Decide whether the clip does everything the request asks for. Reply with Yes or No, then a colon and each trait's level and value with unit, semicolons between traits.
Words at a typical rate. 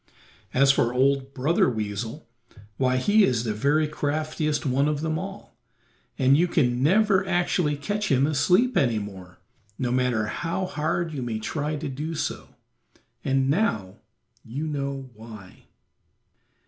Yes: average, 145 wpm